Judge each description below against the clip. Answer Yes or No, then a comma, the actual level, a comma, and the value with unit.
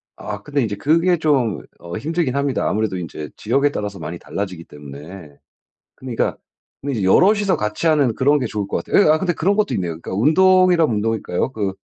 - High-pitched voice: No, low, 120 Hz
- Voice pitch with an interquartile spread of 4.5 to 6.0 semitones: No, wide, 8.4 semitones